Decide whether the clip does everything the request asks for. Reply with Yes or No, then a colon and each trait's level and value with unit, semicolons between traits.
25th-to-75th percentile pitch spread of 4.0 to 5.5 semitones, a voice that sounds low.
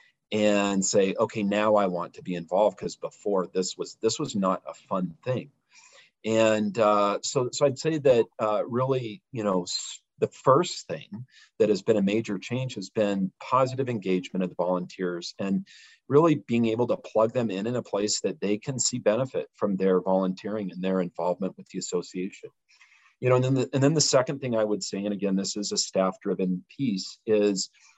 Yes: average, 4.4 semitones; low, 105 Hz